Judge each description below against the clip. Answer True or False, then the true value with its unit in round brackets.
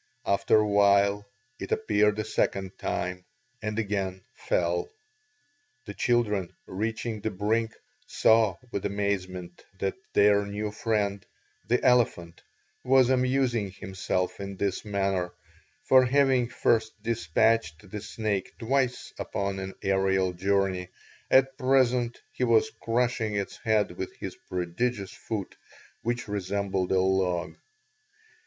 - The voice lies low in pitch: True (105 Hz)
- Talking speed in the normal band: False (120 wpm)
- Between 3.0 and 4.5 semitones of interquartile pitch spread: True (3.3 semitones)